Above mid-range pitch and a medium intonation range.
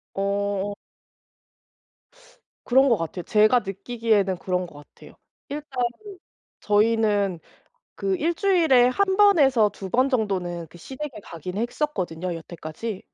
No: high, 210 Hz; wide, 6.0 semitones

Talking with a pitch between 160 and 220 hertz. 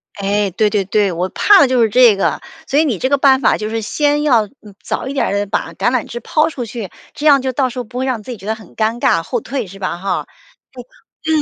No: high, 235 Hz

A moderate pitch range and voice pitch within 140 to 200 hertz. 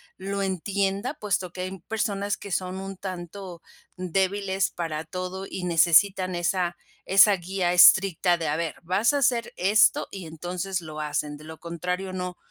No: narrow, 2.1 semitones; medium, 185 Hz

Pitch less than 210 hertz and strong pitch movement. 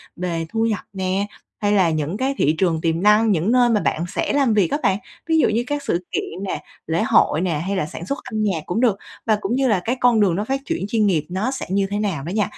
No: high, 200 Hz; average, 4.5 semitones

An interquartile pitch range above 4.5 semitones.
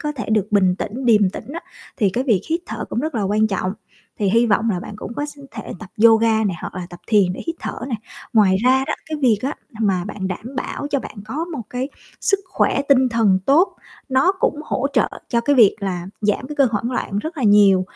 Yes: average, 4.9 semitones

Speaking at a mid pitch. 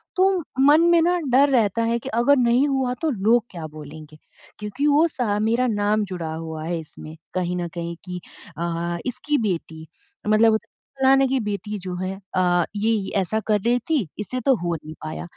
No: high, 210 Hz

